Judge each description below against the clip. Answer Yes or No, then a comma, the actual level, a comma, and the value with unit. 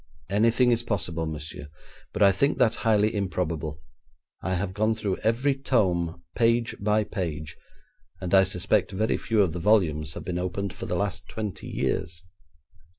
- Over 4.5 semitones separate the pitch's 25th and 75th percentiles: No, average, 4.2 semitones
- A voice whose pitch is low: Yes, very low, 95 Hz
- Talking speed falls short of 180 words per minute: Yes, average, 160 wpm